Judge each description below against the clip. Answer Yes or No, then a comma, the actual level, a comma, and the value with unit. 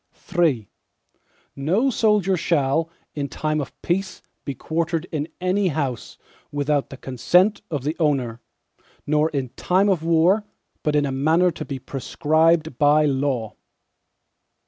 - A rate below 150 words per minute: Yes, slow, 135 wpm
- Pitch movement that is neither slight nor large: Yes, average, 3.9 semitones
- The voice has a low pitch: No, medium, 155 Hz